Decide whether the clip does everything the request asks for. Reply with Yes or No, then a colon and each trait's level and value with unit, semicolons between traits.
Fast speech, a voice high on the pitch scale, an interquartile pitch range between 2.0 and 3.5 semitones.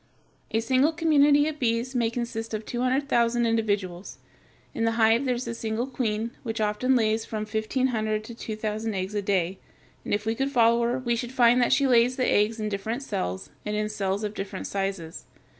Yes: fast, 210 wpm; high, 225 Hz; average, 2.7 semitones